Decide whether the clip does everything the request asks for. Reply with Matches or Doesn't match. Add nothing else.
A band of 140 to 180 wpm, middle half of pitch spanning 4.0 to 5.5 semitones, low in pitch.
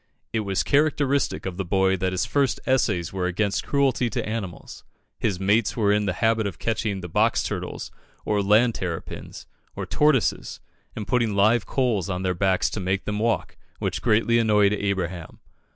Doesn't match